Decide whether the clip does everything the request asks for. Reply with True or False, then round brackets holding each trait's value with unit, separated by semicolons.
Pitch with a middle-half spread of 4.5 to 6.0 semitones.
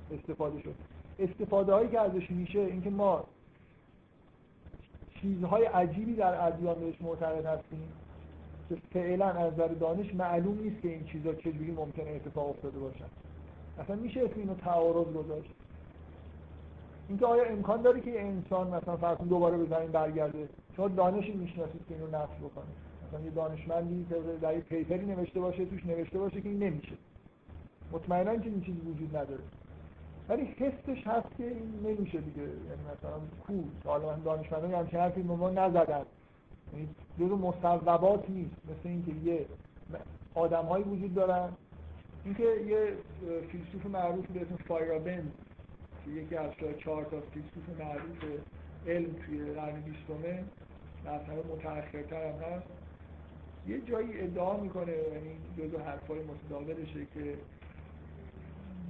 False (4.0 semitones)